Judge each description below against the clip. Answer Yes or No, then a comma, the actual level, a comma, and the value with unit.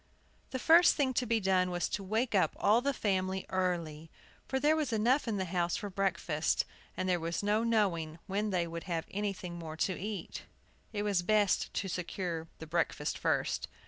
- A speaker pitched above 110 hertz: Yes, high, 190 Hz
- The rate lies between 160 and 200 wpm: Yes, average, 190 wpm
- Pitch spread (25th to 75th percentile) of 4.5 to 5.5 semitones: No, average, 3.9 semitones